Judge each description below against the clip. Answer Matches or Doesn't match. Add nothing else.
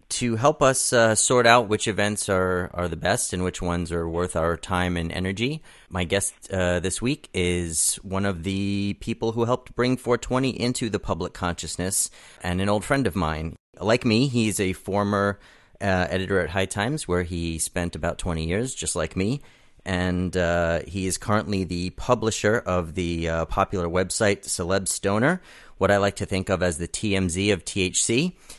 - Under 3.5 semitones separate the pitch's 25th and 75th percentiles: Doesn't match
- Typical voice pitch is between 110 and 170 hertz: Doesn't match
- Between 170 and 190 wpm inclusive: Matches